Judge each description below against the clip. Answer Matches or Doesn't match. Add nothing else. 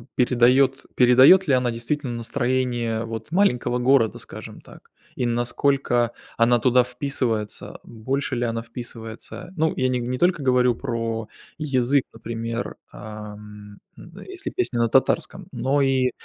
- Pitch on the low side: Matches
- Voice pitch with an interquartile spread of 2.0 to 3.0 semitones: Matches